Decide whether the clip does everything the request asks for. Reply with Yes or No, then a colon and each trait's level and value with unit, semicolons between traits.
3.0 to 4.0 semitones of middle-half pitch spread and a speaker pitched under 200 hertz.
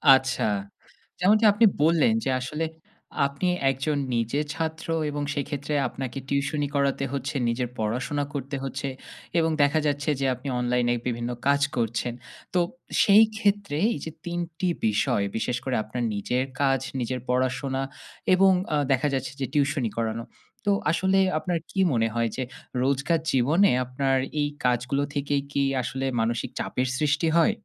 Yes: average, 3.4 semitones; medium, 140 Hz